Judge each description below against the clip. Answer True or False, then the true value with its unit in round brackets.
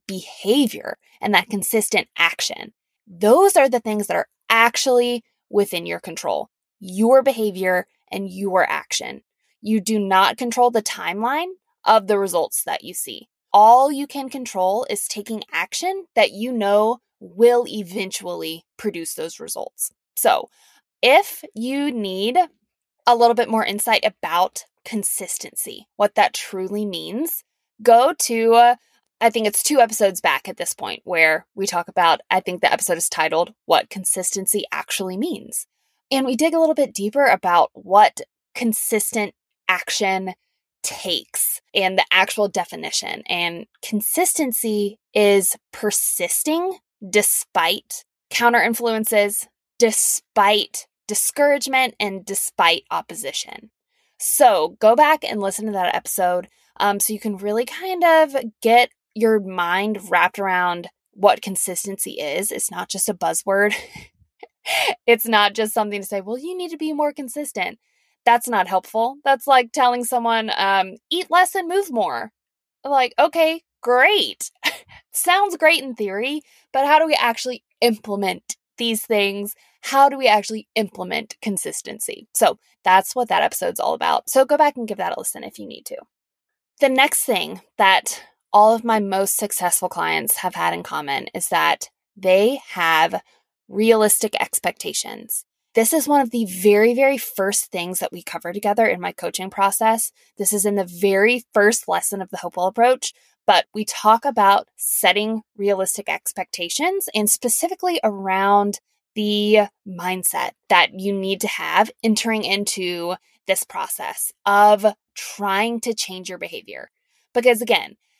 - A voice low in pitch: False (215 Hz)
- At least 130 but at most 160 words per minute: True (145 wpm)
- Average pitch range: True (4.5 semitones)